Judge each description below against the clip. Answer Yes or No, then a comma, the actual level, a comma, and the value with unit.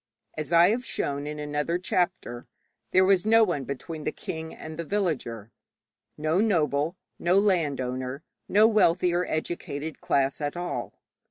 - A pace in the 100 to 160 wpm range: Yes, average, 150 wpm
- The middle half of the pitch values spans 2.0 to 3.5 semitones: No, average, 4.1 semitones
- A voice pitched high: No, medium, 160 Hz